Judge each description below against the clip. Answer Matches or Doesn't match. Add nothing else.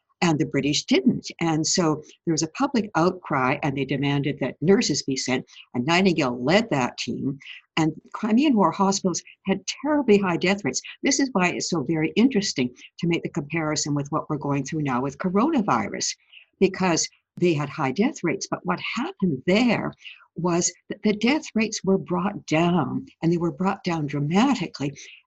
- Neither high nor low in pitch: Matches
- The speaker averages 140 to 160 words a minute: Doesn't match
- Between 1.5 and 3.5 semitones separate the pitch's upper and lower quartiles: Doesn't match